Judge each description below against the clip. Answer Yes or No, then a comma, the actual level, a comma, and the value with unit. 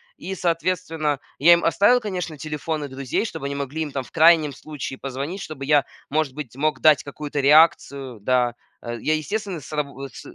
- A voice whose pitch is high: No, medium, 150 Hz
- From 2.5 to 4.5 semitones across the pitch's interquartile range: Yes, average, 3.1 semitones